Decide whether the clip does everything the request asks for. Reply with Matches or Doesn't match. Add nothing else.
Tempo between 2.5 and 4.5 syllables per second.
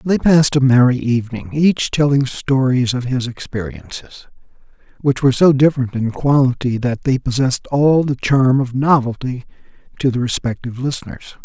Doesn't match